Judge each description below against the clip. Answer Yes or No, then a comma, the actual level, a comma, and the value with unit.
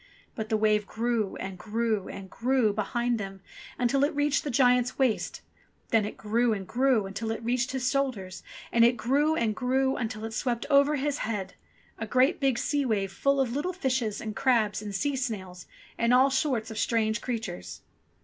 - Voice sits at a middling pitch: No, high, 235 Hz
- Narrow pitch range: No, average, 3.6 semitones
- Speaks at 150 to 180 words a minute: No, average, 190 wpm